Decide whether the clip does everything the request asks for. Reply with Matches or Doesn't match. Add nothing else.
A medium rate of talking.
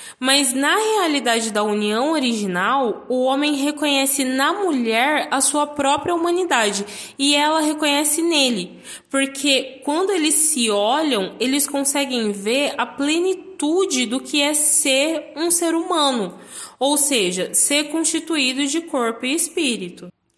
Matches